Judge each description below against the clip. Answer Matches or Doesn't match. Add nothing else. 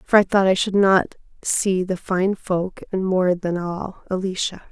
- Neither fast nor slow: Matches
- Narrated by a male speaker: Doesn't match